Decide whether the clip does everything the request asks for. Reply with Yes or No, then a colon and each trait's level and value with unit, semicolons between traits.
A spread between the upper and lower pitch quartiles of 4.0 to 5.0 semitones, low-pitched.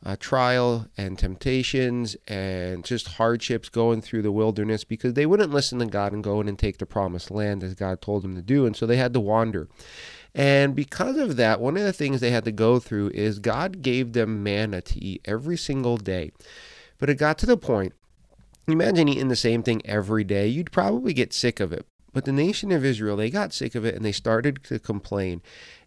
Yes: average, 4.6 semitones; low, 115 Hz